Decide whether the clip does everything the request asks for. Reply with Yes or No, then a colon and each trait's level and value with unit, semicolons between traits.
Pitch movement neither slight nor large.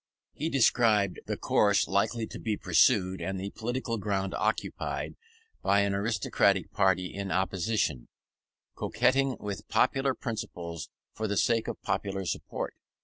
Yes: average, 3.3 semitones